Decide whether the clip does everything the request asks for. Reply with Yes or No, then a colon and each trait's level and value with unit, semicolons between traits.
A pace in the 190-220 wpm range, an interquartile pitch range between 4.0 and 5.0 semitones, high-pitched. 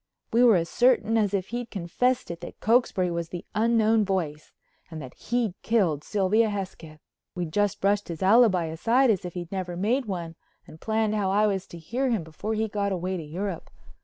Yes: average, 200 wpm; average, 4.3 semitones; high, 195 Hz